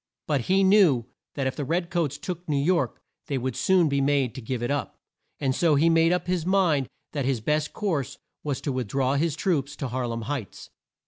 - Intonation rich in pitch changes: No, average, 4.3 semitones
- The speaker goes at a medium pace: No, fast, 220 wpm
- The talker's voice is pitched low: No, medium, 145 Hz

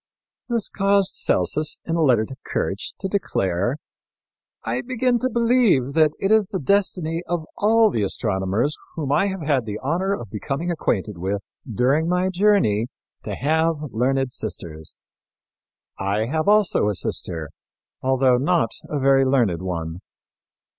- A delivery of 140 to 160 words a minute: Yes, average, 145 wpm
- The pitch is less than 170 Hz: Yes, medium, 140 Hz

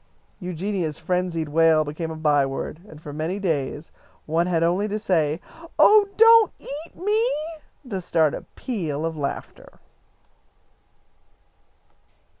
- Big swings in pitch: No, average, 4.5 semitones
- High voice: No, medium, 165 Hz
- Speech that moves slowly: Yes, slow, 120 wpm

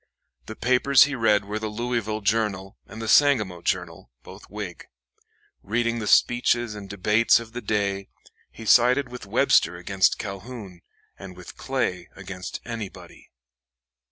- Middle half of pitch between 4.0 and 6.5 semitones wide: No, average, 3.4 semitones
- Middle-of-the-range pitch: No, low, 110 Hz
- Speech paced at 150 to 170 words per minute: No, average, 140 wpm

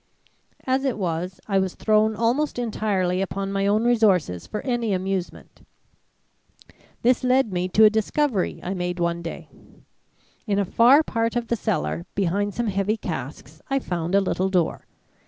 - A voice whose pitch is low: No, high, 200 Hz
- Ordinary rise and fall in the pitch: Yes, average, 4.2 semitones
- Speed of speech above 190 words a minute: No, average, 160 wpm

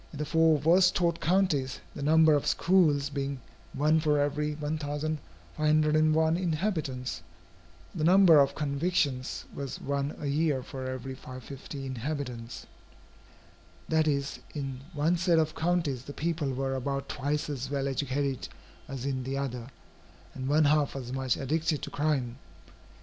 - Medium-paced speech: Yes, average, 145 wpm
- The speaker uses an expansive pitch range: No, average, 2.7 semitones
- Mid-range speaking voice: Yes, medium, 145 Hz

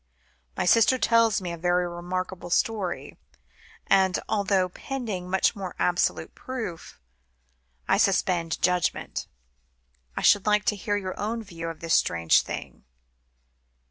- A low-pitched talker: No, medium, 185 Hz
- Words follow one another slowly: Yes, slow, 130 wpm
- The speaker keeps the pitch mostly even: No, average, 3.1 semitones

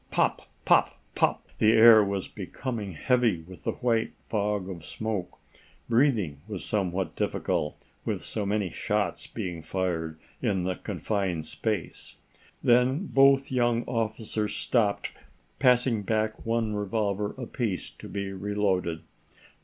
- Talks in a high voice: No, low, 105 Hz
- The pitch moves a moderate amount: Yes, average, 3.7 semitones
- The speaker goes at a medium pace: No, slow, 125 wpm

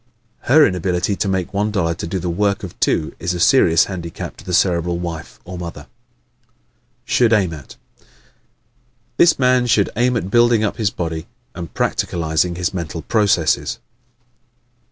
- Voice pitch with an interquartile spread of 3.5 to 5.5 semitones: Yes, average, 3.9 semitones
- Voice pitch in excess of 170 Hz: No, very low, 90 Hz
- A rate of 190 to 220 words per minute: No, average, 155 wpm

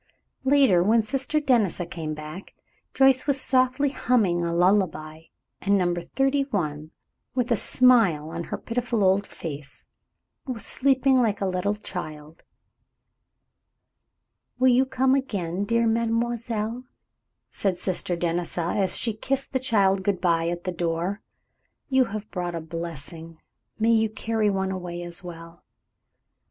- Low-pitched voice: No, high, 200 Hz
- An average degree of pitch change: No, wide, 6.0 semitones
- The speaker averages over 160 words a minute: No, average, 140 wpm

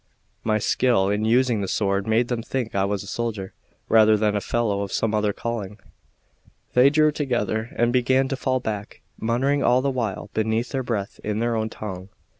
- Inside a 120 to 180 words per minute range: No, average, 195 wpm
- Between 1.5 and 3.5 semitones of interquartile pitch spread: Yes, average, 3.2 semitones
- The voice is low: Yes, low, 110 Hz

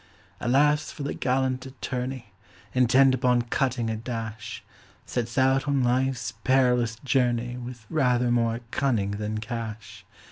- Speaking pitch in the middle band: No, low, 125 Hz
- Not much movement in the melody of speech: Yes, narrow, 2.3 semitones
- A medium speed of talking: No, slow, 130 wpm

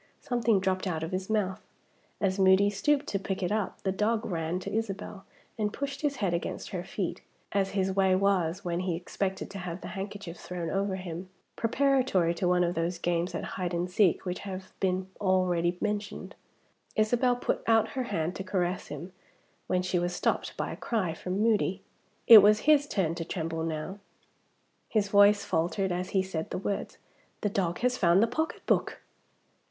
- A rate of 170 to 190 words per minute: Yes, average, 185 wpm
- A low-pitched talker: No, high, 190 Hz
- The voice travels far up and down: No, average, 2.8 semitones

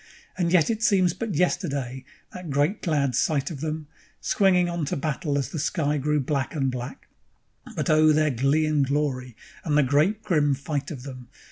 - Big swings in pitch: No, average, 3.6 semitones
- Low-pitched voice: No, medium, 150 Hz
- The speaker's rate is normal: Yes, average, 190 wpm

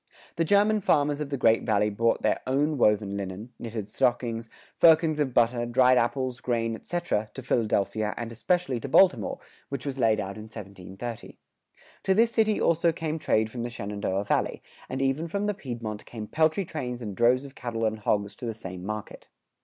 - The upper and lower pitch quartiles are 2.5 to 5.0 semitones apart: No, wide, 5.6 semitones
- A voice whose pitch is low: Yes, low, 120 Hz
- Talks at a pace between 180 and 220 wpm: Yes, average, 185 wpm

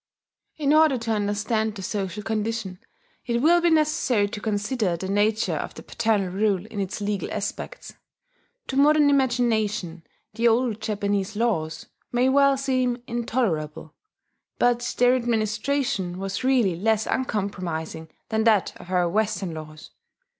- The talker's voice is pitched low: No, high, 220 Hz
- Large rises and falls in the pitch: No, average, 4.1 semitones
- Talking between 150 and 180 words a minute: No, average, 140 wpm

